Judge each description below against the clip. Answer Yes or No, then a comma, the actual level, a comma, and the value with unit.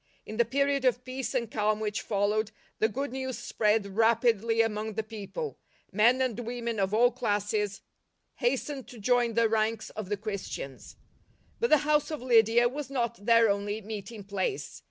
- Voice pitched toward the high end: Yes, high, 225 Hz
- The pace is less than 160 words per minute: No, average, 175 wpm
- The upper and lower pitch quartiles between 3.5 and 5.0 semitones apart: No, average, 3.0 semitones